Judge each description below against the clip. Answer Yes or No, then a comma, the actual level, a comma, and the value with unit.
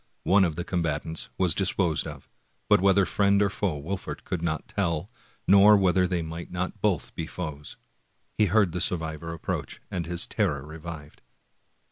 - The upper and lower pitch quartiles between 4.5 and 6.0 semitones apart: No, average, 3.3 semitones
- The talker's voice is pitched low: Yes, very low, 90 Hz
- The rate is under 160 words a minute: No, average, 170 wpm